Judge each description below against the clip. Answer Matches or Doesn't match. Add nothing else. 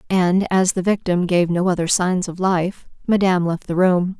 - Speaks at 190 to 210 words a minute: Matches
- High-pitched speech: Doesn't match